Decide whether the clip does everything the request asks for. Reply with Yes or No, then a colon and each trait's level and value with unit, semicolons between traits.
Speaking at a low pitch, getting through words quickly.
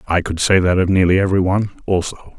Yes: very low, 95 Hz; fast, 225 wpm